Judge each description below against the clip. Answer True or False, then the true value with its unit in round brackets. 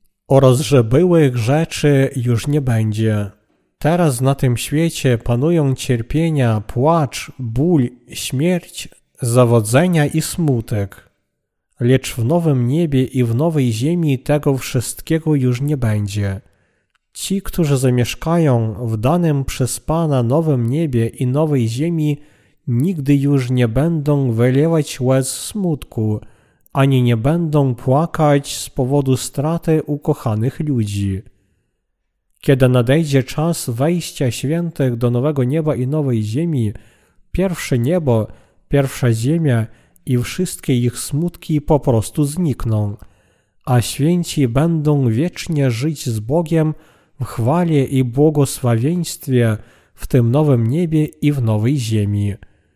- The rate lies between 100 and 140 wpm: True (115 wpm)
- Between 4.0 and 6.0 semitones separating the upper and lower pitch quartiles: True (4.4 semitones)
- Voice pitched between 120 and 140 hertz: True (135 Hz)